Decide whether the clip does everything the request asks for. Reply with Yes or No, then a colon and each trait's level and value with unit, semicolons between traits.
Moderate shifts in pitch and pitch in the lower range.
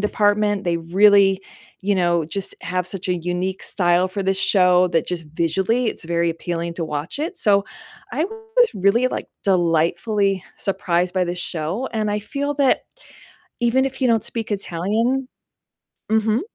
No: average, 4.1 semitones; high, 195 Hz